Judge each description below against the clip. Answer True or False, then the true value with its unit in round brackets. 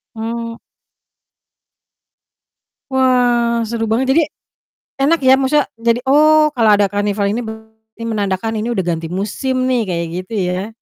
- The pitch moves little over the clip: False (3.7 semitones)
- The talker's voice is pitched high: True (230 Hz)